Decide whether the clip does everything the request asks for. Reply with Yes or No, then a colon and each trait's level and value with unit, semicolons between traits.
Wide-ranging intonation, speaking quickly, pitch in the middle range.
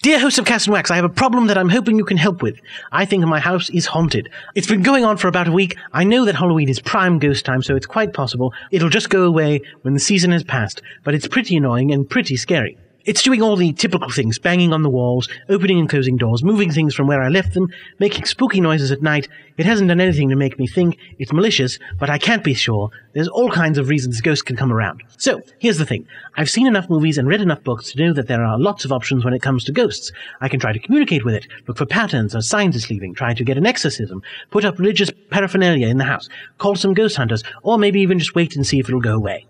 Yes: wide, 6.9 semitones; fast, 265 wpm; medium, 155 Hz